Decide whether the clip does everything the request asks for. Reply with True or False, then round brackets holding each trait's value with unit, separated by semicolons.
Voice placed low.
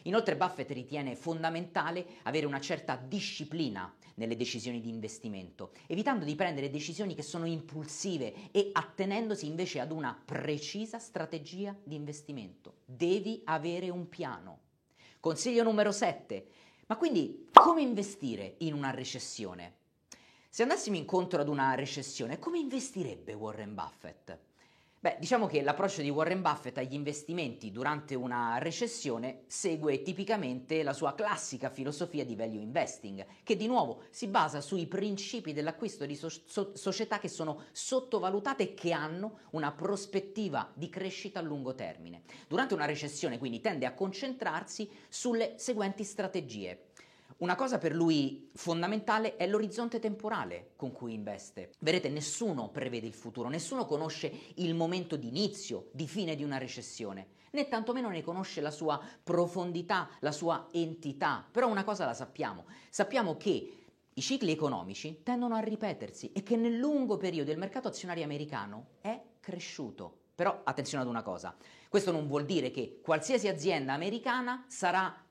False (165 Hz)